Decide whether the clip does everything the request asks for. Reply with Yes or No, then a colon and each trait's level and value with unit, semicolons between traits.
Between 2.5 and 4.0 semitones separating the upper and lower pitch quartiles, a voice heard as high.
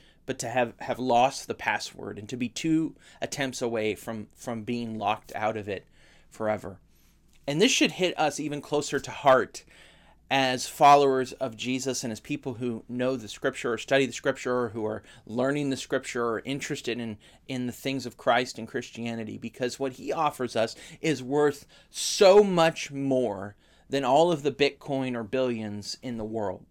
No: average, 3.5 semitones; low, 130 Hz